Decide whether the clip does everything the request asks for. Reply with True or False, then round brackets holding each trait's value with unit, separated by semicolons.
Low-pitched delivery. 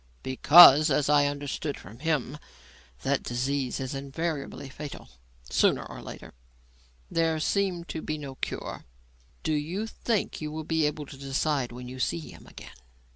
False (145 Hz)